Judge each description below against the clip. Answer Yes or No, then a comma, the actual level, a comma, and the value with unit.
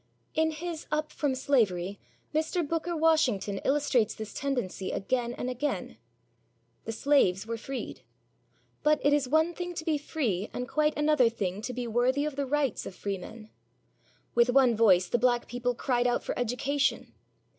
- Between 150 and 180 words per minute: Yes, average, 165 wpm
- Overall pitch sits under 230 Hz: No, very high, 255 Hz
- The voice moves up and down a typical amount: Yes, average, 4.7 semitones